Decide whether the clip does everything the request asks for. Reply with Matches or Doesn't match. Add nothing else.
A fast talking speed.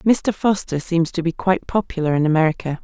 Doesn't match